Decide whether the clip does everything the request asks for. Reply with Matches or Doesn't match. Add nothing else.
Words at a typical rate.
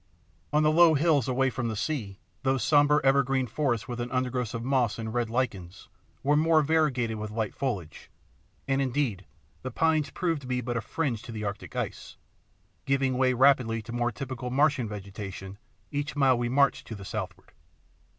Matches